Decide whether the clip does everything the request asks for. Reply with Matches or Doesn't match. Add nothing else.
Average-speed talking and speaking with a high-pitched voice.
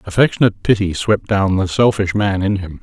Doesn't match